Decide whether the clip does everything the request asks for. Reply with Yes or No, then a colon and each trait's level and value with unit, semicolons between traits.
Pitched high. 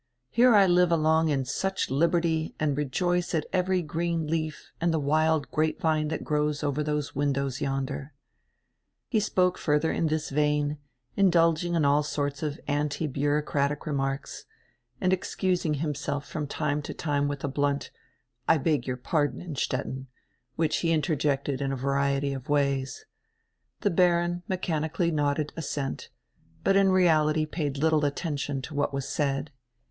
No: medium, 150 Hz